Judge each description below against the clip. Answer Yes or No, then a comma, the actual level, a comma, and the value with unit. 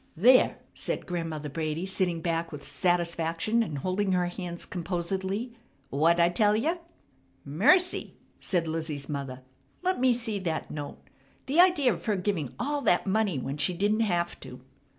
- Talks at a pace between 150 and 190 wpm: Yes, average, 155 wpm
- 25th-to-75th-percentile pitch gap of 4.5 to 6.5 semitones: Yes, average, 4.8 semitones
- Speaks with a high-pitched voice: No, medium, 180 Hz